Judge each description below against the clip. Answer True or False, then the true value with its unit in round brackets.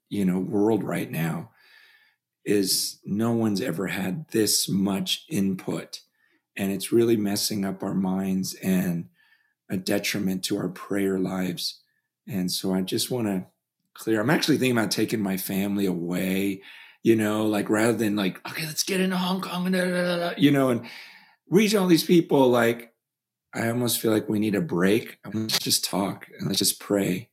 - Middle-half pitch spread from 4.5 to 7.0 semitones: True (4.9 semitones)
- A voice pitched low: True (105 Hz)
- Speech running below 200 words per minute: True (175 wpm)